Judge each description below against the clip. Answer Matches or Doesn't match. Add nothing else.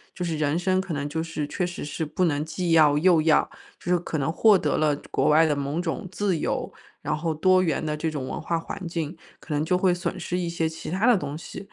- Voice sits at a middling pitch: Matches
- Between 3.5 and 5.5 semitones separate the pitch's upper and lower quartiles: Doesn't match